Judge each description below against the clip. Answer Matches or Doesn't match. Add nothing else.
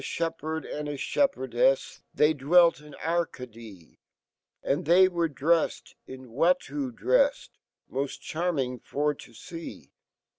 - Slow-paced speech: Matches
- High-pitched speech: Doesn't match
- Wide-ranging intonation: Doesn't match